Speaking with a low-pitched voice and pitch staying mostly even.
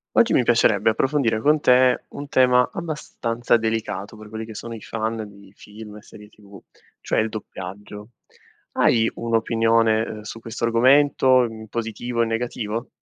Yes: low, 115 Hz; narrow, 2.1 semitones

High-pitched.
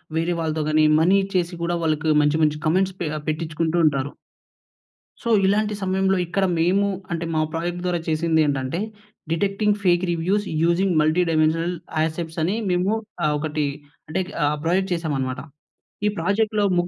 No: medium, 170 Hz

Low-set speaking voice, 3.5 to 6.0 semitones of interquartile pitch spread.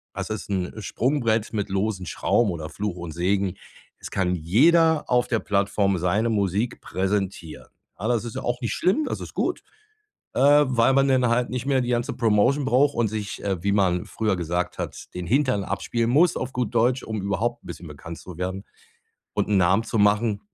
Yes: low, 105 Hz; average, 4.4 semitones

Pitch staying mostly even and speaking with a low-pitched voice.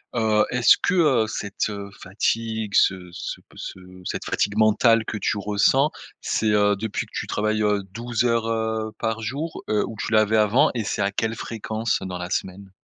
Yes: narrow, 1.8 semitones; low, 110 Hz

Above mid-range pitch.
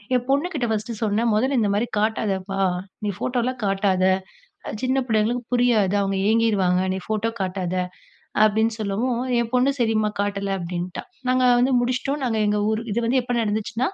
Yes: high, 220 Hz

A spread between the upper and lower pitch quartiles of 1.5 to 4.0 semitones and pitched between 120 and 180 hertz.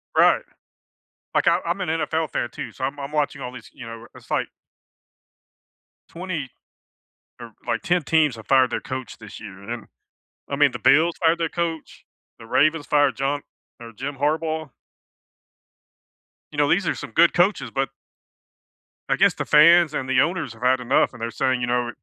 No: average, 4.5 semitones; medium, 140 Hz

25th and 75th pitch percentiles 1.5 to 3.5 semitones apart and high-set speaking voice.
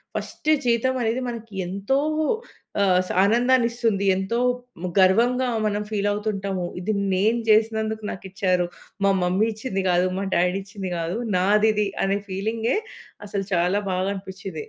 Yes: average, 2.9 semitones; high, 200 Hz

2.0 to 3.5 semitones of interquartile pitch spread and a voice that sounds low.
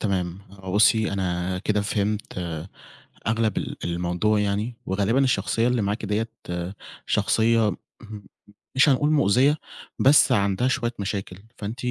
Yes: average, 3.1 semitones; low, 105 Hz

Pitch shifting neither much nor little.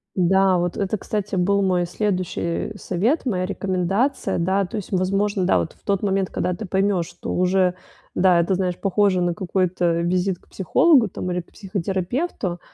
No: narrow, 1.9 semitones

